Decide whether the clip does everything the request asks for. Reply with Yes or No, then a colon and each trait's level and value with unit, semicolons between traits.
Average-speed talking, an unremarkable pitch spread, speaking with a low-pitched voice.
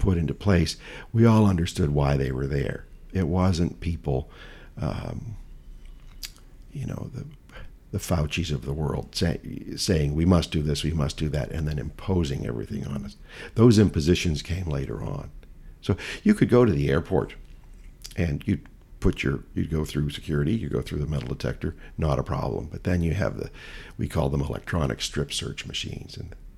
Yes: average, 180 wpm; average, 4.9 semitones; very low, 80 Hz